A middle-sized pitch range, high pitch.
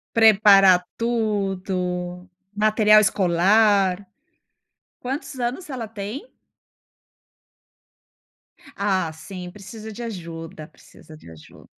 Yes: average, 3.5 semitones; high, 200 Hz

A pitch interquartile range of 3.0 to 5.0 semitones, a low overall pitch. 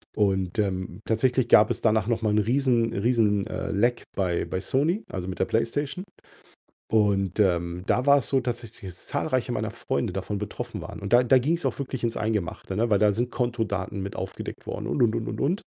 Yes: average, 3.8 semitones; low, 110 Hz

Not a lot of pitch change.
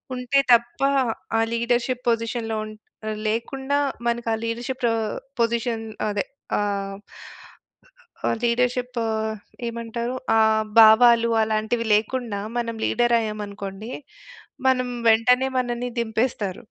Yes: narrow, 1.8 semitones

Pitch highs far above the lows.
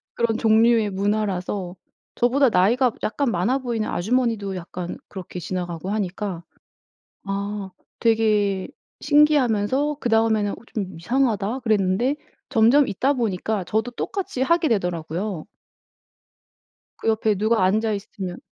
No: average, 3.9 semitones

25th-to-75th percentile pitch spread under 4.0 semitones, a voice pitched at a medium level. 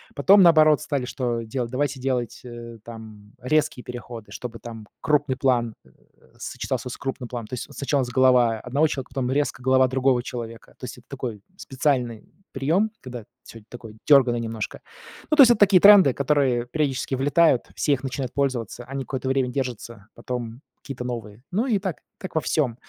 No: average, 3.0 semitones; low, 130 Hz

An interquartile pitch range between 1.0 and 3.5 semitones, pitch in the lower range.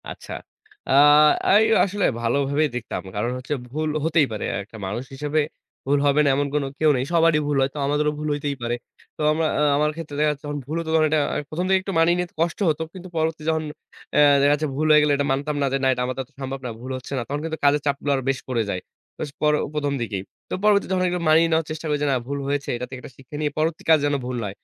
No: average, 2.7 semitones; medium, 145 Hz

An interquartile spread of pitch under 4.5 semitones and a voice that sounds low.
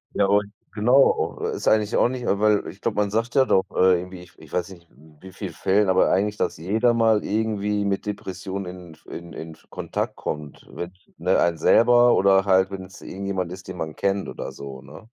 Yes: narrow, 2.6 semitones; very low, 95 Hz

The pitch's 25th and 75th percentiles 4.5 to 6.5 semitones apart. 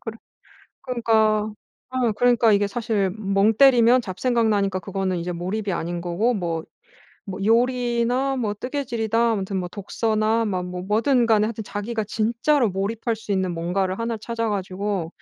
No: average, 3.3 semitones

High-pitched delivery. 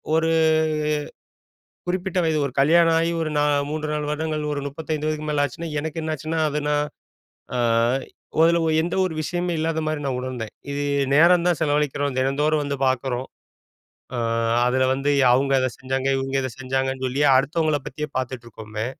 No: medium, 150 Hz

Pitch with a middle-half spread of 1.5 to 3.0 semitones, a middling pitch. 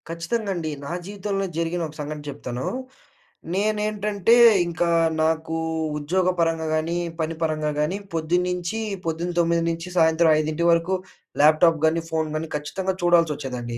Yes: narrow, 2.4 semitones; medium, 165 Hz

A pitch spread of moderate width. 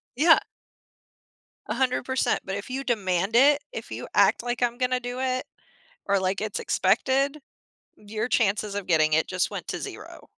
Yes: average, 4.7 semitones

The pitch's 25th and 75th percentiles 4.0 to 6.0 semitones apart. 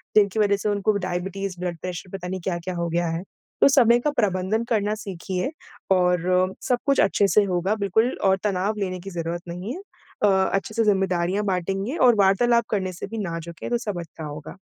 No: average, 2.9 semitones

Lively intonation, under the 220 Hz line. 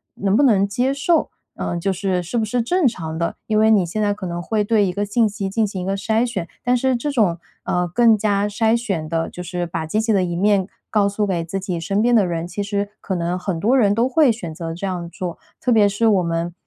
No: average, 3.8 semitones; high, 200 Hz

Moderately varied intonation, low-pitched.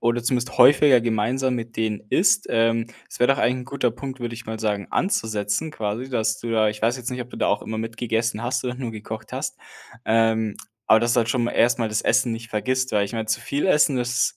No: narrow, 2.3 semitones; low, 115 Hz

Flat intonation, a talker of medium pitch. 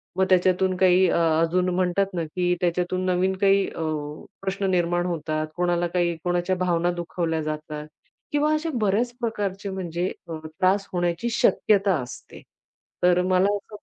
Yes: narrow, 1.8 semitones; medium, 180 Hz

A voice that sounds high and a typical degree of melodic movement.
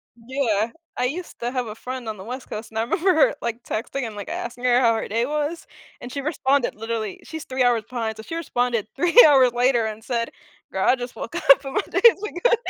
Yes: high, 245 Hz; average, 3.3 semitones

